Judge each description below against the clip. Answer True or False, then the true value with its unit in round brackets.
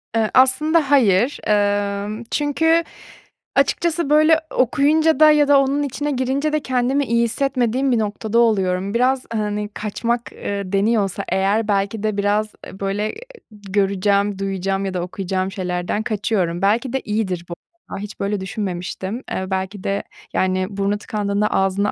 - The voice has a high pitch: True (210 Hz)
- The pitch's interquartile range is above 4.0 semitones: True (4.7 semitones)